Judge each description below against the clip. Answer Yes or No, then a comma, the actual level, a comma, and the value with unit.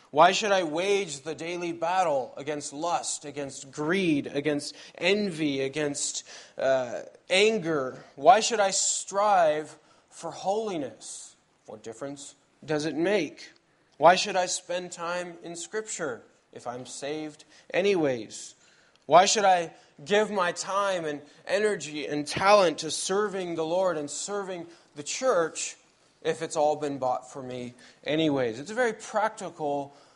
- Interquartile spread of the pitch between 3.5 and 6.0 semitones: Yes, average, 4.7 semitones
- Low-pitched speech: No, medium, 165 Hz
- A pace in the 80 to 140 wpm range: Yes, slow, 135 wpm